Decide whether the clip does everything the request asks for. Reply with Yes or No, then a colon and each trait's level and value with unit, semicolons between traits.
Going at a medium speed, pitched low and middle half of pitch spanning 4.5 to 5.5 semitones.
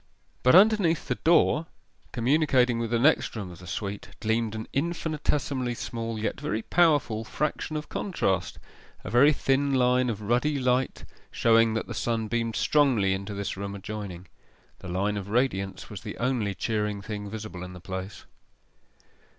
Yes: average, 160 wpm; low, 115 Hz; average, 4.8 semitones